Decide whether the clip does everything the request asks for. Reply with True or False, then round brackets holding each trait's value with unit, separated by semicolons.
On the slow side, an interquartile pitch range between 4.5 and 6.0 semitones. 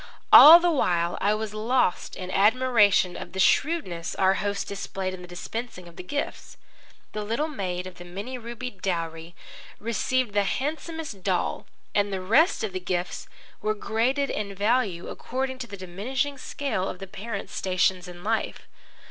False (170 wpm; 5.4 semitones)